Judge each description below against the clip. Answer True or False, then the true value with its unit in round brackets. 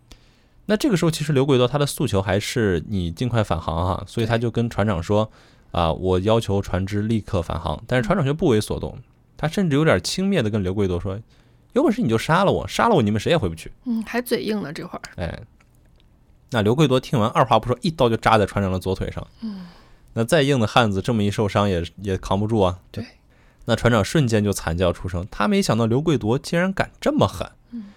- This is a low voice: True (115 Hz)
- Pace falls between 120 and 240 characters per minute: False (330 characters per minute)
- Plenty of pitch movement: True (6.7 semitones)